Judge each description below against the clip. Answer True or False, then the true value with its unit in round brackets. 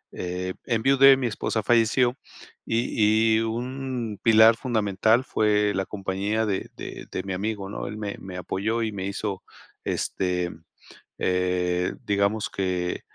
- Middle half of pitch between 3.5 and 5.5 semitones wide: False (3.0 semitones)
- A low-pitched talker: True (105 Hz)